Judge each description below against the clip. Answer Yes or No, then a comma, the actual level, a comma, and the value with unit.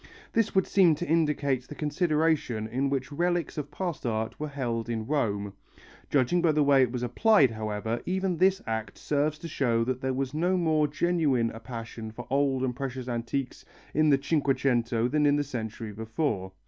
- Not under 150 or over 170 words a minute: No, average, 185 wpm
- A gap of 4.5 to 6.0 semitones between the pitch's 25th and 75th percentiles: Yes, average, 4.8 semitones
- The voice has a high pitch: No, low, 135 Hz